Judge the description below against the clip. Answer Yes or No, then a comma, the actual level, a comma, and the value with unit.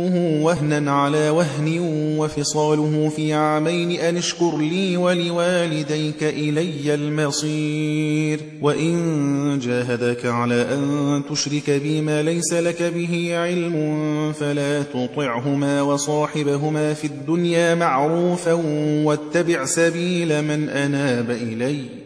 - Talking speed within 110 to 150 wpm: No, average, 95 wpm